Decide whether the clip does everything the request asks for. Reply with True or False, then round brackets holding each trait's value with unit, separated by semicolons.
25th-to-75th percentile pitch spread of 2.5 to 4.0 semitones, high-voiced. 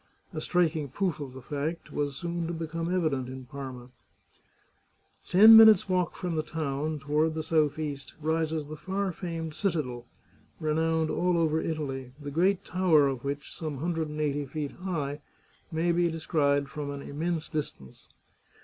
False (2.9 semitones; 155 Hz)